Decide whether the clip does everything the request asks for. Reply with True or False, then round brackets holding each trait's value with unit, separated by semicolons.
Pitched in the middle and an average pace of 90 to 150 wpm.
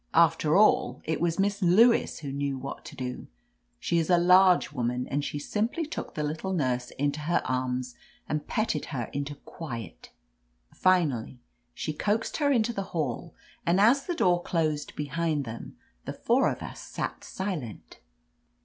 False (155 Hz; 165 wpm)